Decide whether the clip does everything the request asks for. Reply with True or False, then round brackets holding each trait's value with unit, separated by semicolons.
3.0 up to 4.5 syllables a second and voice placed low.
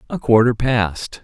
True (3.8 syllables/s; 120 Hz)